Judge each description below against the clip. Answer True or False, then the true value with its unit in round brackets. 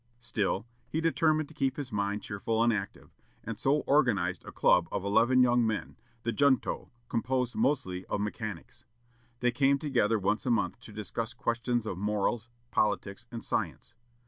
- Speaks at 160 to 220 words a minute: True (165 wpm)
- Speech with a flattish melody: False (3.9 semitones)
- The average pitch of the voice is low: True (115 Hz)